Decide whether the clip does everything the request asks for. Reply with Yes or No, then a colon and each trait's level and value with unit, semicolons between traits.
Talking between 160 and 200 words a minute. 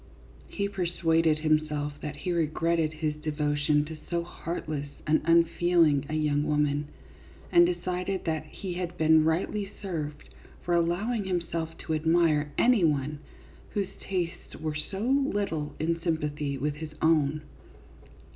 No: slow, 135 wpm